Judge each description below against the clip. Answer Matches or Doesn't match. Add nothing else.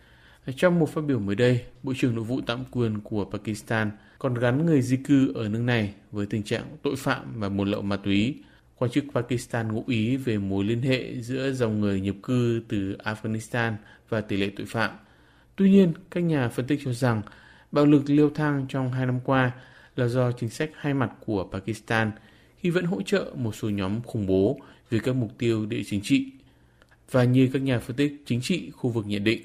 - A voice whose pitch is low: Matches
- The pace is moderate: Matches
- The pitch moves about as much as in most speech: Matches